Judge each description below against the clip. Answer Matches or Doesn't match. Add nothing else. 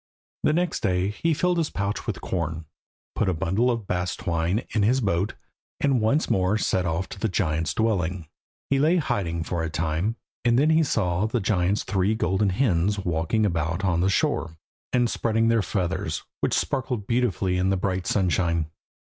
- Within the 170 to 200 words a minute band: Matches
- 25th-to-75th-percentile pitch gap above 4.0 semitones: Matches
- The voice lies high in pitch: Doesn't match